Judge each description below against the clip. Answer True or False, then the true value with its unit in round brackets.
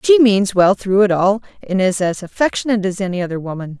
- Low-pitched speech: False (200 Hz)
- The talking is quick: True (220 wpm)